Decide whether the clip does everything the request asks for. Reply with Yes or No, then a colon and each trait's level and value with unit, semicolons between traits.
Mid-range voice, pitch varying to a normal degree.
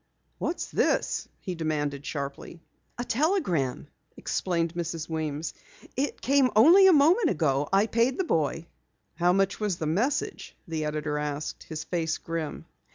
No: medium, 170 Hz; wide, 7.6 semitones